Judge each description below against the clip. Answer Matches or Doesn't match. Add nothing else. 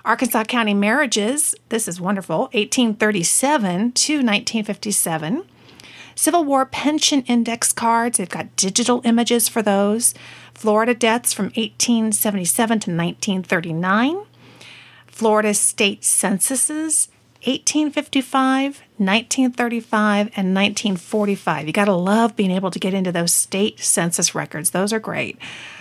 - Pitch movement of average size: Matches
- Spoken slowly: Matches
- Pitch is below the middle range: Doesn't match